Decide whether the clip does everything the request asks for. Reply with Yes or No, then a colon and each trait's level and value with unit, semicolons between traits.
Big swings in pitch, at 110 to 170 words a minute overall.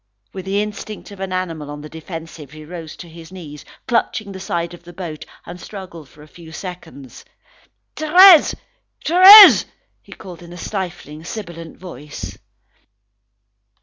No: average, 3.4 semitones; average, 150 wpm